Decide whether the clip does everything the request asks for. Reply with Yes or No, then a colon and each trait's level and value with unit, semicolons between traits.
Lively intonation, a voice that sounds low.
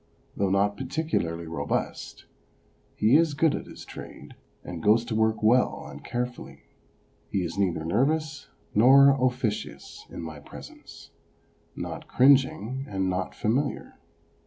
Yes: wide, 5.9 semitones; low, 115 Hz